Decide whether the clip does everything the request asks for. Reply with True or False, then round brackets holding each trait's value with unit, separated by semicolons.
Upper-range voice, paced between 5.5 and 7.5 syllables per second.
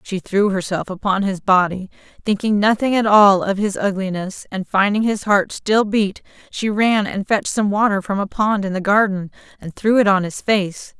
False (200 Hz; 4.8 syllables/s)